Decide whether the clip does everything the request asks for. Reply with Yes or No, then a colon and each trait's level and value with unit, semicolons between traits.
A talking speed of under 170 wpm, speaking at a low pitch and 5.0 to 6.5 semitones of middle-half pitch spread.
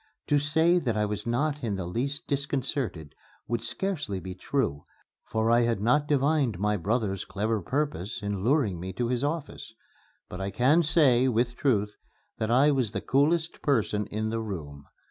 No: average, 175 wpm; low, 120 Hz; wide, 5.6 semitones